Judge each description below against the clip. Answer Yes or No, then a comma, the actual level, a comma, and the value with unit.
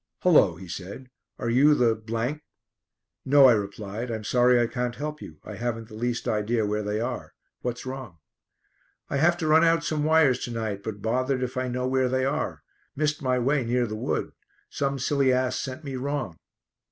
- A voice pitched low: Yes, low, 125 Hz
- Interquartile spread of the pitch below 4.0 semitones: Yes, average, 3.6 semitones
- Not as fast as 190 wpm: No, average, 195 wpm